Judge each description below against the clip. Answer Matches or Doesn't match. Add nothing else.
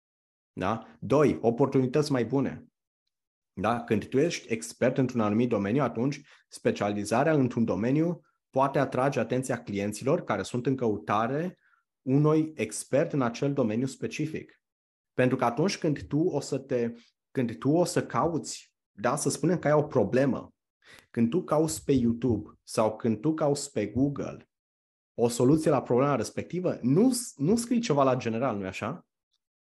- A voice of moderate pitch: Doesn't match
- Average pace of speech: Matches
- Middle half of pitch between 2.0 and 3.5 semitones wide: Doesn't match